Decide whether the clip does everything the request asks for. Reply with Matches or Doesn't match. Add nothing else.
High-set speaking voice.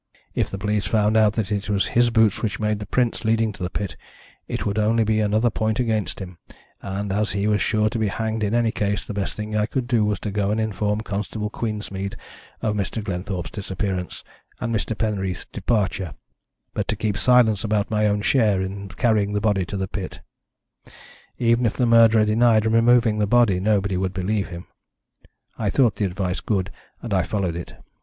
Doesn't match